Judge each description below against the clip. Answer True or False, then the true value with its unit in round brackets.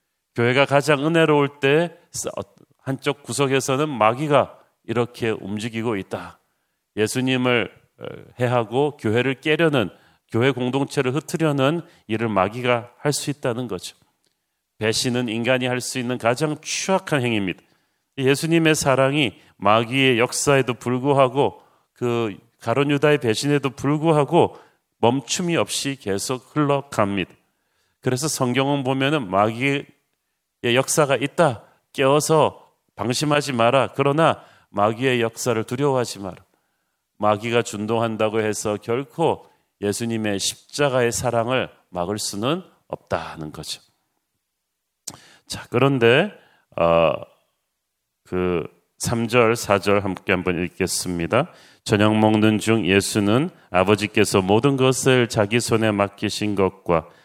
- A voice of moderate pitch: False (120 Hz)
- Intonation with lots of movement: False (4.8 semitones)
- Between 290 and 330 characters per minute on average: False (255 characters per minute)